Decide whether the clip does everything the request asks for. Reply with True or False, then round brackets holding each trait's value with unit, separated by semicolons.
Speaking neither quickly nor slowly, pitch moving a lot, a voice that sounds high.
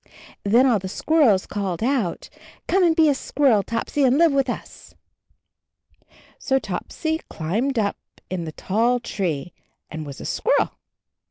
True (150 wpm; 6.8 semitones; 230 Hz)